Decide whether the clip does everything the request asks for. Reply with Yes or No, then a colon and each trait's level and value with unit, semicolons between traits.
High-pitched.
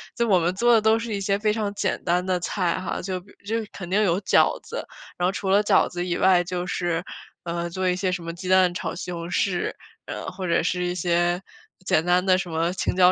No: medium, 180 Hz